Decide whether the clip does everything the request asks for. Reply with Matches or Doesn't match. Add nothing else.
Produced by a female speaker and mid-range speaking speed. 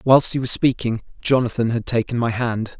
Doesn't match